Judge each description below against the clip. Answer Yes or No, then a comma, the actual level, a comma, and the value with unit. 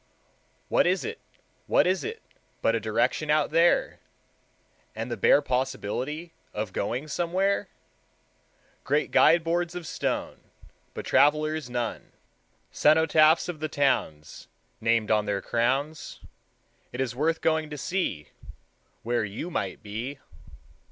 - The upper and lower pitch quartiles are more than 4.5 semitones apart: Yes, wide, 5.6 semitones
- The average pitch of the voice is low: No, medium, 145 Hz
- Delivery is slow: Yes, slow, 125 wpm